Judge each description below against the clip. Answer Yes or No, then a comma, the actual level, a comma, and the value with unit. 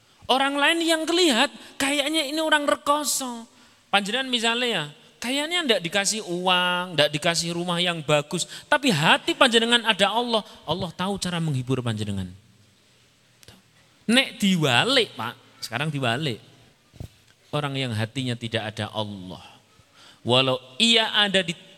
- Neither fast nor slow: Yes, average, 125 wpm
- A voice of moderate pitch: Yes, medium, 180 Hz